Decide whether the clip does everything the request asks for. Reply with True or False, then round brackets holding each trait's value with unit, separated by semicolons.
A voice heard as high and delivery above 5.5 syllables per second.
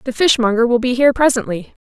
True (245 Hz; 6.6 syllables/s)